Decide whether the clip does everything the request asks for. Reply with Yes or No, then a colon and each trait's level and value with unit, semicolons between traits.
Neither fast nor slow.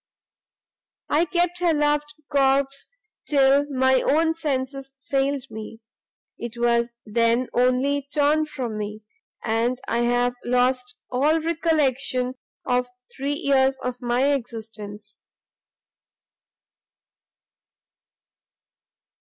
No: slow, 95 wpm